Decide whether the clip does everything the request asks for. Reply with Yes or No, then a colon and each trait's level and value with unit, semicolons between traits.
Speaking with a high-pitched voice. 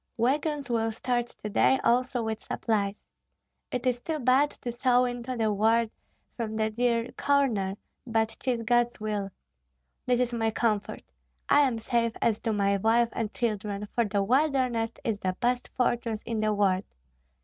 Yes: high, 230 Hz